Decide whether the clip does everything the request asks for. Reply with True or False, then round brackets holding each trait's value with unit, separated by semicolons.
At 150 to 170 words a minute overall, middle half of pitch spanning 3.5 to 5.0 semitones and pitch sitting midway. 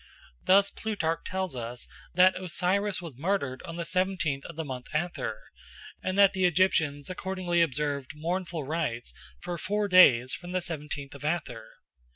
True (155 wpm; 4.7 semitones; 170 Hz)